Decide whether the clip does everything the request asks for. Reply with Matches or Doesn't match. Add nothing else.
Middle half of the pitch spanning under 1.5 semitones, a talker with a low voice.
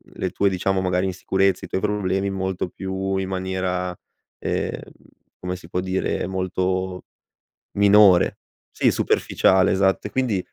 Matches